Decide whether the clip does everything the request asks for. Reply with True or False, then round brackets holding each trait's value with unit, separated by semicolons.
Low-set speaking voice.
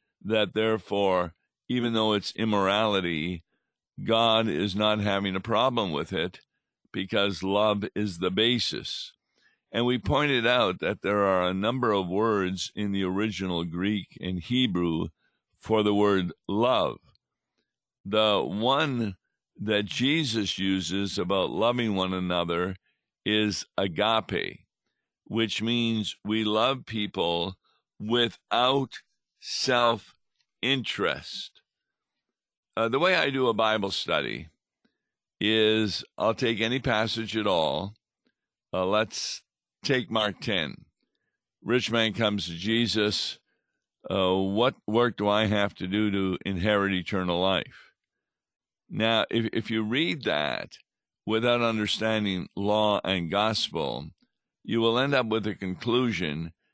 True (105 Hz)